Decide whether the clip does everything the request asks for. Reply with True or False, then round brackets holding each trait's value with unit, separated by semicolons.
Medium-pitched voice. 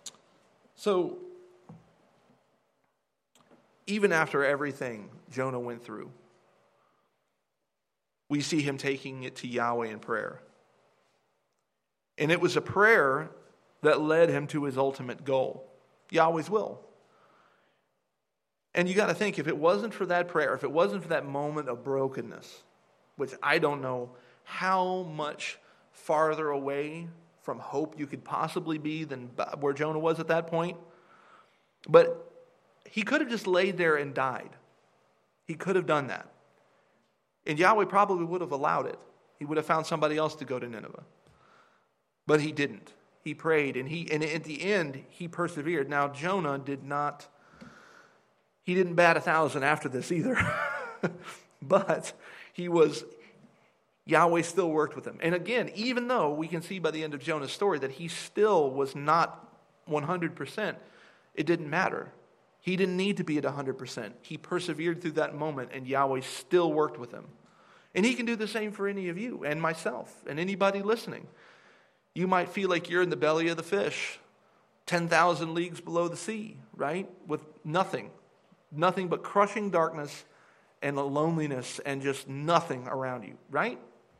True (160 Hz)